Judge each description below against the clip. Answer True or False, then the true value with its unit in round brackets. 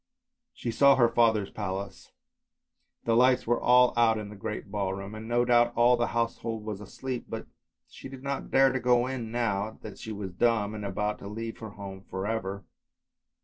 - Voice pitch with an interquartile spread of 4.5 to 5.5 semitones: False (2.9 semitones)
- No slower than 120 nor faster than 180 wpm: False (190 wpm)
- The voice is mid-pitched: False (115 Hz)